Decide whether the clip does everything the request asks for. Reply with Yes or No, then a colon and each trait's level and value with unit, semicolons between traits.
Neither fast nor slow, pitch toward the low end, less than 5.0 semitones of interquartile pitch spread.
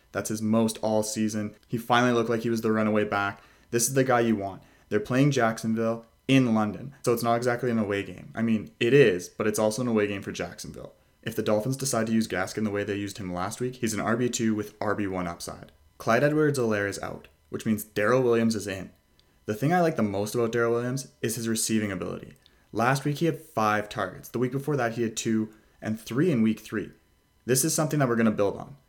No: fast, 240 wpm; low, 110 Hz; narrow, 2.5 semitones